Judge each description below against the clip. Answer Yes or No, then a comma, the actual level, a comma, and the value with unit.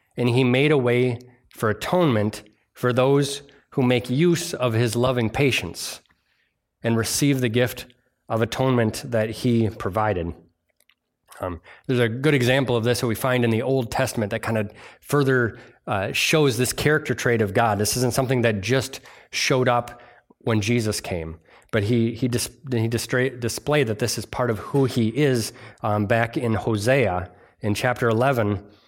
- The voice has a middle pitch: No, low, 120 Hz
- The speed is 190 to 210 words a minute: No, average, 170 wpm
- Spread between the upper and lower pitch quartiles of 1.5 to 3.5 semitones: Yes, average, 2.7 semitones